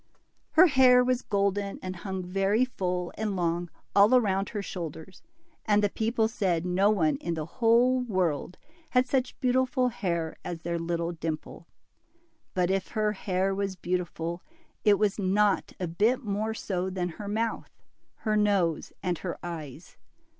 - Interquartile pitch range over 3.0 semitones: Yes, average, 3.8 semitones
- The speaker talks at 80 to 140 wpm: No, average, 155 wpm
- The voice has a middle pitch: No, high, 195 Hz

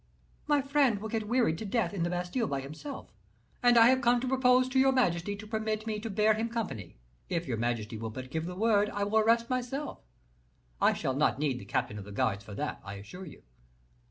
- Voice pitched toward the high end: Yes, high, 210 Hz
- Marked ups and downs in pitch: Yes, wide, 8.8 semitones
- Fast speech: Yes, fast, 235 wpm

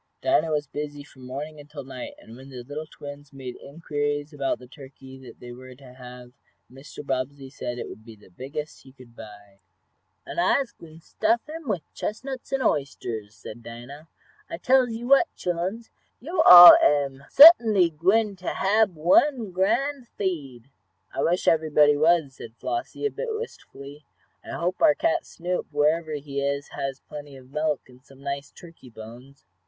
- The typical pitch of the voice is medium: Yes, medium, 145 Hz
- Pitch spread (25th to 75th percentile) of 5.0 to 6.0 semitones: Yes, wide, 5.6 semitones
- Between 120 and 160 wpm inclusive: No, average, 170 wpm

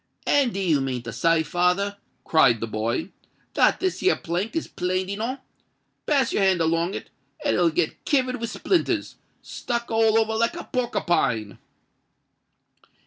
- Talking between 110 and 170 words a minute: Yes, average, 150 wpm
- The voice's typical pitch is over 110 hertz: Yes, high, 190 Hz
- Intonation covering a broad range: Yes, wide, 6.3 semitones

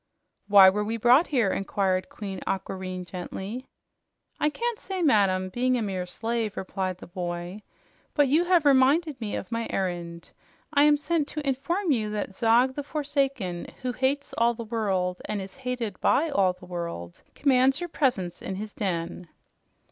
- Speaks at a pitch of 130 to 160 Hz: No, high, 225 Hz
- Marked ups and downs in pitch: Yes, wide, 6.6 semitones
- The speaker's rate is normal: Yes, average, 170 wpm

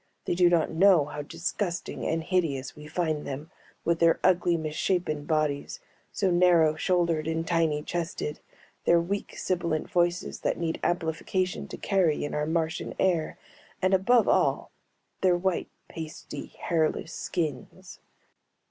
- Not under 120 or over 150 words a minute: Yes, average, 140 wpm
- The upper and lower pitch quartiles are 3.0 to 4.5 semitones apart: No, narrow, 2.4 semitones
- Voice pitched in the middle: Yes, medium, 165 Hz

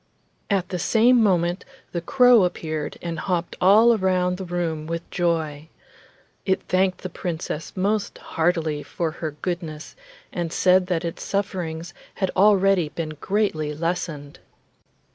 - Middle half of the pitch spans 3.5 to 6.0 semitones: No, average, 2.9 semitones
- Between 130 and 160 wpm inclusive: Yes, slow, 135 wpm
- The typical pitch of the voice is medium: Yes, medium, 175 Hz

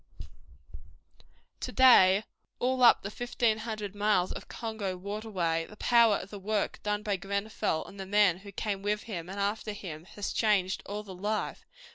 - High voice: Yes, high, 205 Hz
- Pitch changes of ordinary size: No, narrow, 2.1 semitones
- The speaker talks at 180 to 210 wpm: No, average, 170 wpm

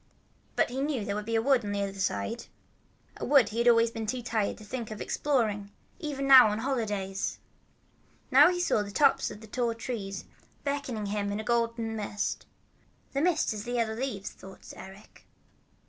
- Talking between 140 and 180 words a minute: No, average, 195 wpm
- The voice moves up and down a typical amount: Yes, average, 3.7 semitones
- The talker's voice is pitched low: No, high, 225 Hz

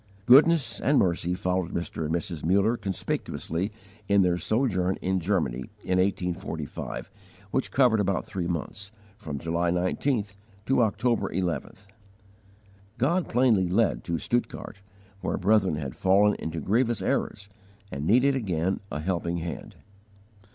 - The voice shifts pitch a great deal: No, average, 4.3 semitones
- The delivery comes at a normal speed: No, slow, 130 wpm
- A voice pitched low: Yes, very low, 95 Hz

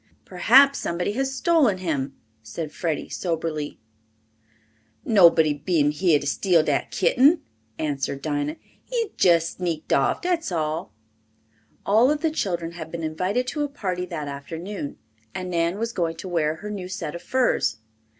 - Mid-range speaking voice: Yes, medium, 175 Hz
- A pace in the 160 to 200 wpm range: No, average, 150 wpm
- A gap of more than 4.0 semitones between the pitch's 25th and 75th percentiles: Yes, average, 5.1 semitones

